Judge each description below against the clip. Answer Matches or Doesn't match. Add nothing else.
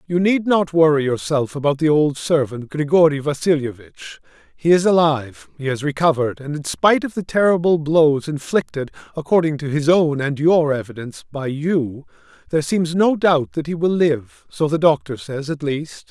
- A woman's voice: Doesn't match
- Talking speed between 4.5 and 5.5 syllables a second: Matches